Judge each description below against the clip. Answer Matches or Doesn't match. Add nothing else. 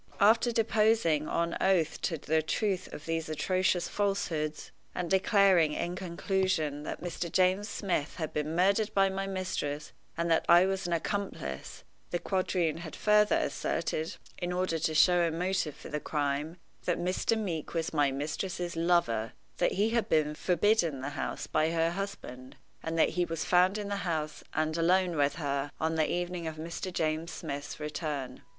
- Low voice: Doesn't match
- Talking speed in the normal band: Matches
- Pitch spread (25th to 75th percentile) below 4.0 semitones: Matches